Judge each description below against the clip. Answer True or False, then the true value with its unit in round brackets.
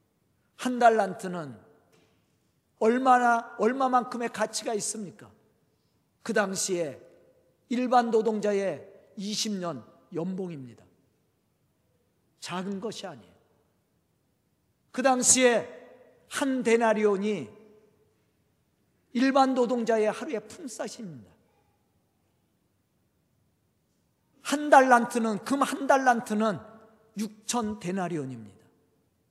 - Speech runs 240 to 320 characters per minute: False (180 characters per minute)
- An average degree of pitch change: True (5.0 semitones)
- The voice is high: True (215 Hz)